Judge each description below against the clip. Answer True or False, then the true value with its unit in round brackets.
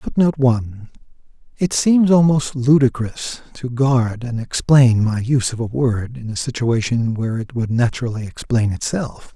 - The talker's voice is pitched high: False (125 Hz)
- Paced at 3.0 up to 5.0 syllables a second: True (4.7 syllables/s)